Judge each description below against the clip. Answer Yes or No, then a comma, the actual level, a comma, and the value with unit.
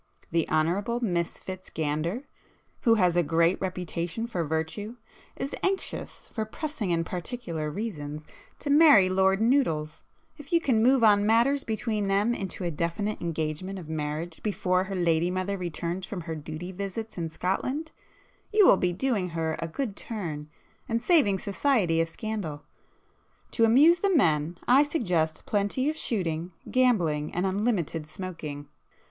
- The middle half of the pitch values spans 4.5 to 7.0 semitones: Yes, wide, 5.6 semitones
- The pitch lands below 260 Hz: Yes, medium, 185 Hz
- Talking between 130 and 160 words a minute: Yes, average, 150 wpm